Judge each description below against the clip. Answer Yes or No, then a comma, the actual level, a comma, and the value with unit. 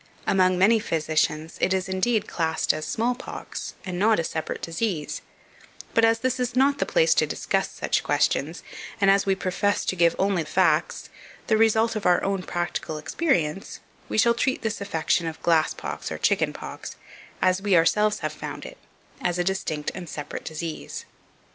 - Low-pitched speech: No, high, 190 Hz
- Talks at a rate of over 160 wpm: Yes, average, 180 wpm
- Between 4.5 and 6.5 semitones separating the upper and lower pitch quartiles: Yes, average, 5.0 semitones